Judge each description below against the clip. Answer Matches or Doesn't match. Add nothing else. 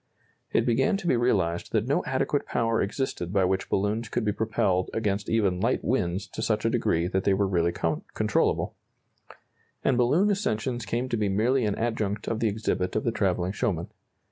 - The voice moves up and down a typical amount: Matches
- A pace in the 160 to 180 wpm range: Doesn't match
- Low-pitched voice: Matches